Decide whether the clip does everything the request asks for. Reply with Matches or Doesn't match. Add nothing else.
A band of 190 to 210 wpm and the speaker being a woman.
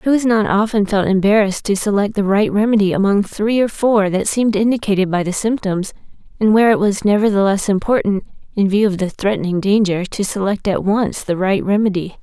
Matches